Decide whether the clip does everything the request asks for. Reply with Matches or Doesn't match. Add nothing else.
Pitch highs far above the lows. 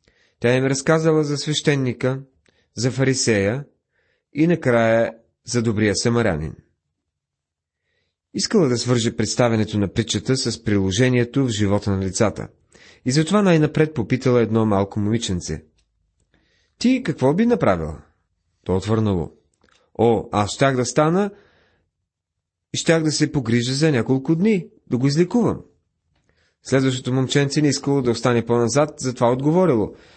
Matches